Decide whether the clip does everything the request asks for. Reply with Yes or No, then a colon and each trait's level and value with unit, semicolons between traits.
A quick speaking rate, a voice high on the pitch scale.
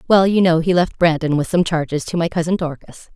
No: fast, 245 wpm; medium, 170 Hz